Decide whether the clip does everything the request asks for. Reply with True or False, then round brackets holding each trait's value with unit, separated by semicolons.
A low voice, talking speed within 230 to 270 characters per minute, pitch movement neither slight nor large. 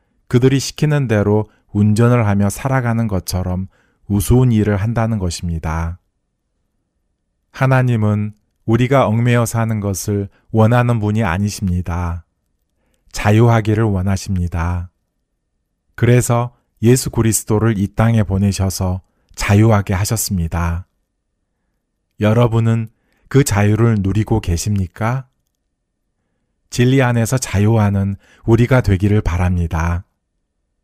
True (105 Hz; 245 characters per minute; 4.2 semitones)